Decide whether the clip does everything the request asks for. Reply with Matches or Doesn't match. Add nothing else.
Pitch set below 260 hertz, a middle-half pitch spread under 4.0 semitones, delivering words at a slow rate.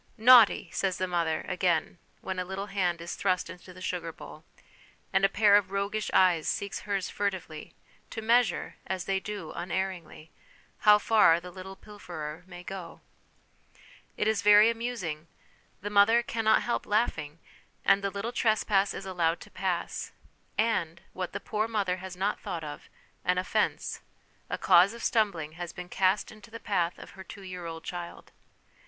Doesn't match